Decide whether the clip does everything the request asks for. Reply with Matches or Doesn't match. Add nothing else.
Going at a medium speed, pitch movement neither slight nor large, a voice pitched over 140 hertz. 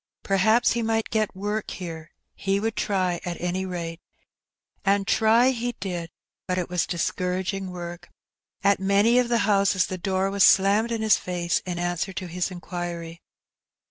Matches